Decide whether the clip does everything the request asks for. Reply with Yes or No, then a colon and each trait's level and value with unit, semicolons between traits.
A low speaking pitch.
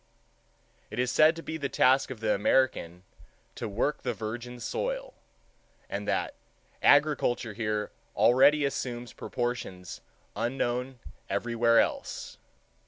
Yes: low, 125 Hz